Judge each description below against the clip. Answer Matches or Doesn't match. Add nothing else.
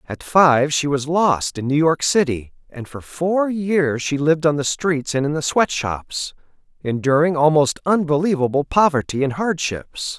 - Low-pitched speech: Doesn't match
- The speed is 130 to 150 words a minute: Doesn't match